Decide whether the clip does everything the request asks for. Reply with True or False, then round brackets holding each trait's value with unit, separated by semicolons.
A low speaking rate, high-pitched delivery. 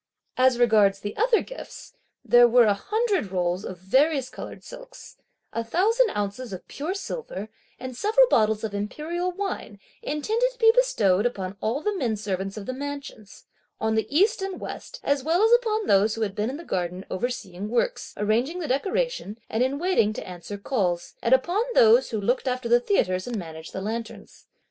False (190 wpm; 245 Hz)